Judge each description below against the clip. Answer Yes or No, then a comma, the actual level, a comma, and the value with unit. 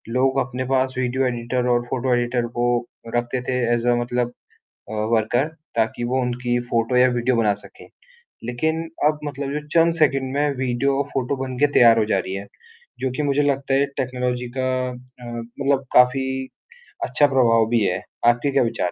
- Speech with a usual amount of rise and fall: No, narrow, 2.0 semitones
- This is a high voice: No, low, 125 Hz